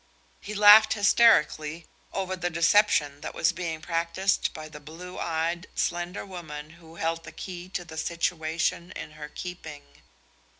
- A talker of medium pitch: Yes, medium, 170 Hz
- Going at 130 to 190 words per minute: Yes, average, 145 wpm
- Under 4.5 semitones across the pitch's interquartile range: Yes, narrow, 2.5 semitones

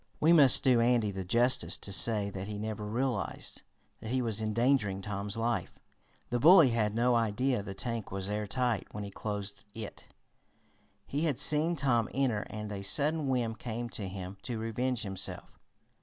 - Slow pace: No, average, 170 wpm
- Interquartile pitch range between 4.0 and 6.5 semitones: No, average, 3.6 semitones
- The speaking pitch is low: Yes, low, 115 Hz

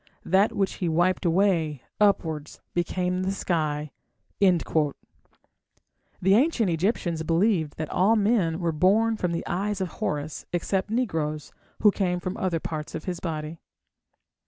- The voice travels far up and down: No, average, 3.5 semitones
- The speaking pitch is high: No, medium, 180 Hz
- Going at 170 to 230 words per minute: No, slow, 135 wpm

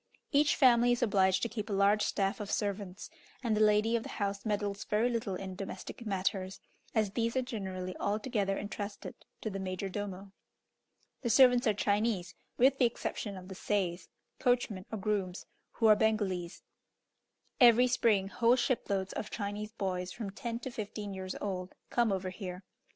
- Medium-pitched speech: No, high, 205 Hz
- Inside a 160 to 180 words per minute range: Yes, average, 170 wpm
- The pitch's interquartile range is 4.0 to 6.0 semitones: No, average, 3.2 semitones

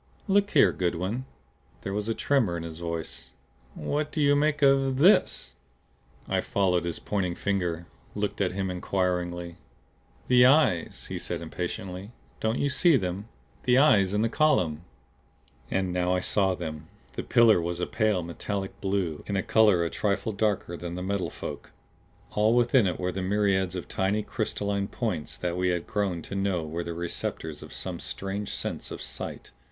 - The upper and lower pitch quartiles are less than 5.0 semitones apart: Yes, average, 3.8 semitones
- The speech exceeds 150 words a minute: Yes, average, 170 wpm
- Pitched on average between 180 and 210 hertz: No, very low, 95 Hz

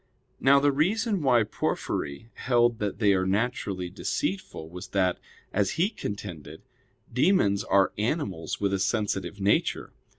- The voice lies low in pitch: Yes, low, 105 Hz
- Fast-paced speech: No, slow, 135 wpm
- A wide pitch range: No, average, 4.9 semitones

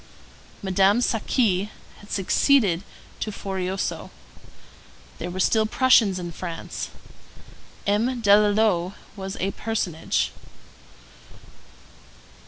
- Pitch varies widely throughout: No, average, 2.9 semitones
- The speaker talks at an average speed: No, slow, 80 wpm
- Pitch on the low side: No, high, 200 Hz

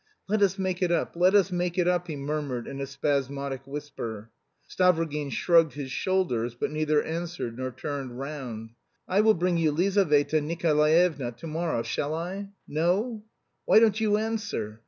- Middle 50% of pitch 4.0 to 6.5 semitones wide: Yes, average, 4.7 semitones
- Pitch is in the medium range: Yes, medium, 155 Hz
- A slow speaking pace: No, average, 170 wpm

